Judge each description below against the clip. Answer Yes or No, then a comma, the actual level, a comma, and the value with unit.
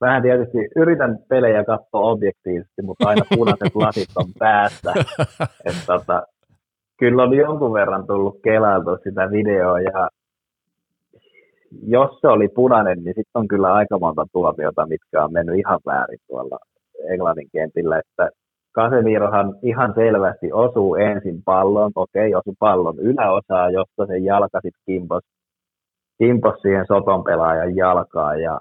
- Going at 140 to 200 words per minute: No, average, 130 wpm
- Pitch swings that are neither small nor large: Yes, average, 3.5 semitones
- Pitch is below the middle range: Yes, low, 100 Hz